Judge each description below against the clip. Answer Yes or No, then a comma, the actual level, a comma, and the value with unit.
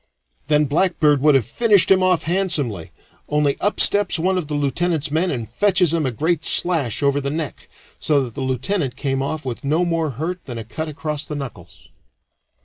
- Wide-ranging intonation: No, average, 4.1 semitones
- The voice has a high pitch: No, medium, 150 Hz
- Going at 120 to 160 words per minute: No, average, 195 wpm